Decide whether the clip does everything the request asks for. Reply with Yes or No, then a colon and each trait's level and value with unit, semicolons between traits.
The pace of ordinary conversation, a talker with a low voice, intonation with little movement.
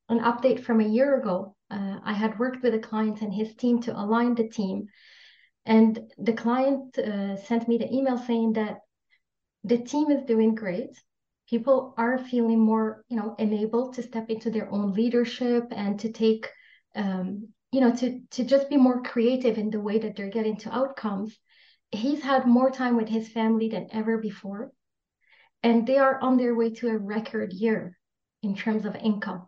No: average, 185 wpm; high, 225 Hz; narrow, 2.2 semitones